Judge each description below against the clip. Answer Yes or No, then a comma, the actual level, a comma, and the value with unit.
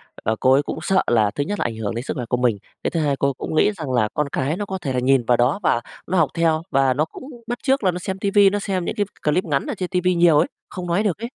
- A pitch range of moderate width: No, wide, 6.4 semitones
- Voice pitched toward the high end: No, medium, 155 Hz